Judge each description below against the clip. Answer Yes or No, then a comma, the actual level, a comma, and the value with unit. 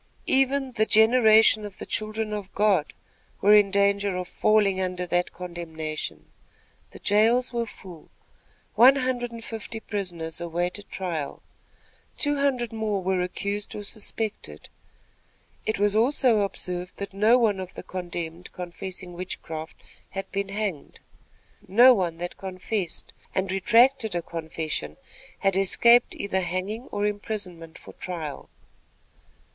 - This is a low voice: No, high, 200 Hz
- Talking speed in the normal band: No, slow, 130 wpm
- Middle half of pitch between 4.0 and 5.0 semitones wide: No, average, 3.6 semitones